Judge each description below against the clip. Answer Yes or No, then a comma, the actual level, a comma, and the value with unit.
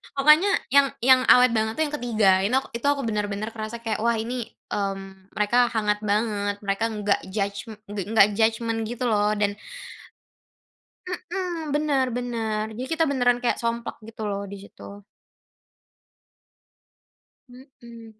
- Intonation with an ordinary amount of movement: Yes, average, 3.3 semitones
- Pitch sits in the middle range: No, high, 225 Hz